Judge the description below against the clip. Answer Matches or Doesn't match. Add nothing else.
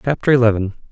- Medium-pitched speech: Doesn't match